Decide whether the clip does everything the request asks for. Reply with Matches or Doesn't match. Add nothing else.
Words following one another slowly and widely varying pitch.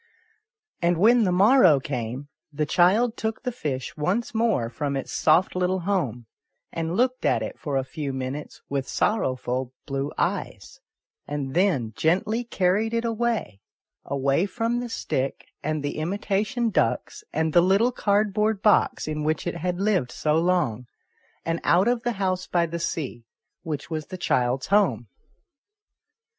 Doesn't match